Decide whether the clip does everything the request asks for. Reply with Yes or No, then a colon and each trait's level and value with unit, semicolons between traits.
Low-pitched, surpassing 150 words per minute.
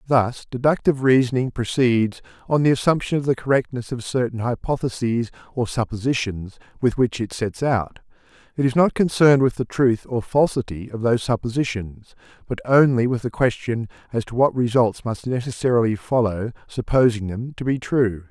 Yes: low, 120 Hz; average, 160 wpm